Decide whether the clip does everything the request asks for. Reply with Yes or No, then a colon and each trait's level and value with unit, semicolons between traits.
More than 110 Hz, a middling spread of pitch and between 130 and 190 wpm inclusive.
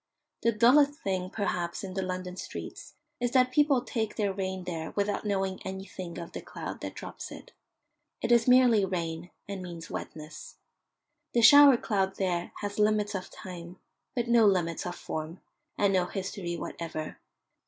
Yes: high, 190 Hz; average, 3.9 semitones; average, 165 wpm